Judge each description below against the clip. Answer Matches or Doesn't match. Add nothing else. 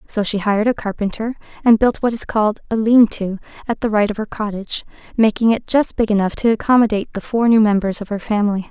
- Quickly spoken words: Matches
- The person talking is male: Doesn't match